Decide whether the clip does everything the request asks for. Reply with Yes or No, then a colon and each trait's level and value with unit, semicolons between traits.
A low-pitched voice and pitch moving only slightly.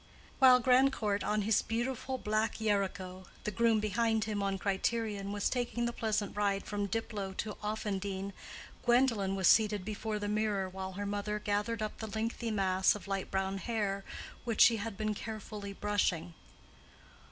No: high, 210 Hz; narrow, 2.1 semitones